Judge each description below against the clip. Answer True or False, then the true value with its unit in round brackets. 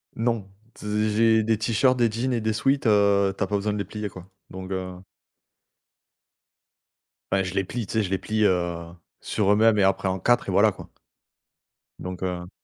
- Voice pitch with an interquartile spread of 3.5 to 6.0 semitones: False (2.9 semitones)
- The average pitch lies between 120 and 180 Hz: False (105 Hz)